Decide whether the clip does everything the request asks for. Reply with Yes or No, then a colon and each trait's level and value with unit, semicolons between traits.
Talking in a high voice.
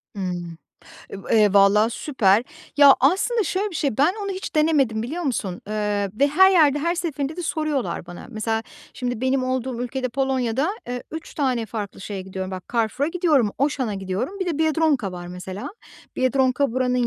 Yes: very high, 255 Hz